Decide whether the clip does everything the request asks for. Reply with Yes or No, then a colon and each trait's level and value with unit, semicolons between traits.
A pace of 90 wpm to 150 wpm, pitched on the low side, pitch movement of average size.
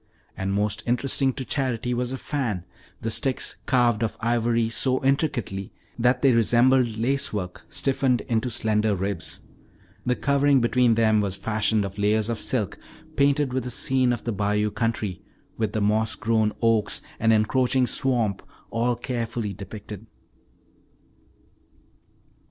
Yes: average, 140 wpm; low, 115 Hz; average, 3.1 semitones